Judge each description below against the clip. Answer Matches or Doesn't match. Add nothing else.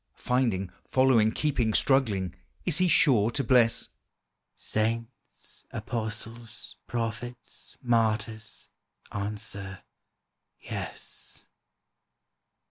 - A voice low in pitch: Matches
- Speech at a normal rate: Doesn't match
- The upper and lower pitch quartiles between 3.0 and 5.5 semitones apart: Doesn't match